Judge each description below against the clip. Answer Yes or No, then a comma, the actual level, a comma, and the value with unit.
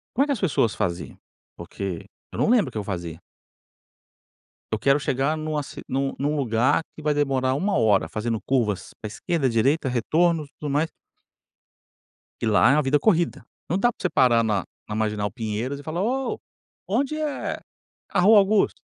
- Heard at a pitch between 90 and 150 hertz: Yes, medium, 140 Hz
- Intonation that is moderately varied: No, wide, 7.1 semitones